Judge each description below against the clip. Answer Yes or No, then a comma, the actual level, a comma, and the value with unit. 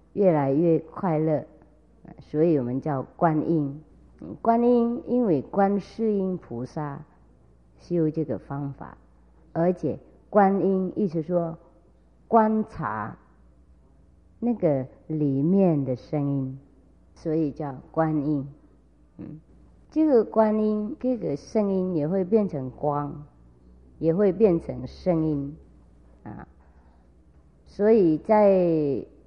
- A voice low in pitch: No, medium, 155 Hz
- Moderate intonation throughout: No, wide, 6.8 semitones